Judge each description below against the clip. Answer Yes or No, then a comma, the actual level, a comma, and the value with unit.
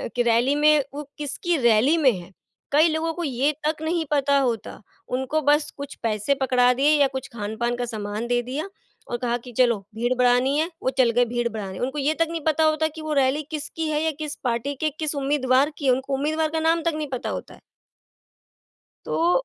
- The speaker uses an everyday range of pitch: Yes, average, 4.1 semitones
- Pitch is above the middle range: Yes, very high, 275 Hz